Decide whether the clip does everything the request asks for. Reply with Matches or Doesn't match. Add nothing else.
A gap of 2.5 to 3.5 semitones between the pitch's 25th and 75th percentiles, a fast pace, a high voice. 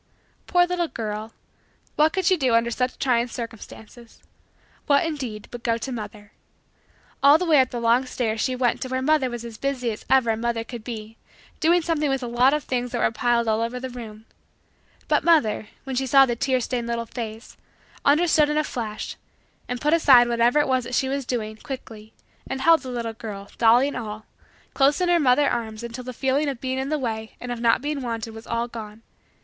Matches